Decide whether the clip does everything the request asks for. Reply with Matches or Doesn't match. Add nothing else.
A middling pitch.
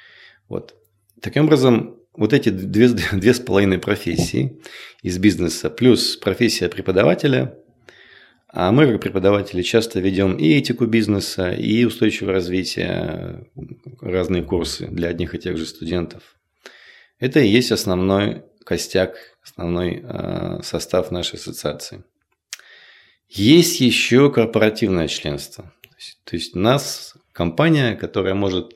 Doesn't match